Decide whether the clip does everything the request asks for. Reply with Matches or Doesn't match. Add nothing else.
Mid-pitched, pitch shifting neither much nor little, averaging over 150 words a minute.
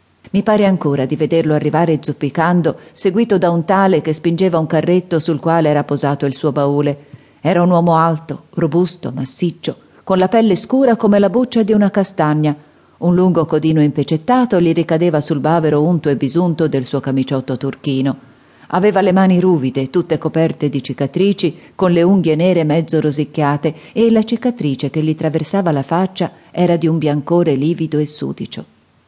Matches